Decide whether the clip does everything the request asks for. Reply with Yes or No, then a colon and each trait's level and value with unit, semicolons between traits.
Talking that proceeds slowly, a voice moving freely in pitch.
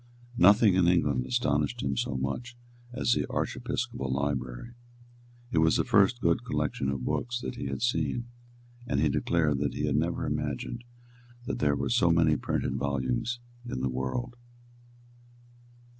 No: average, 155 wpm; wide, 8.6 semitones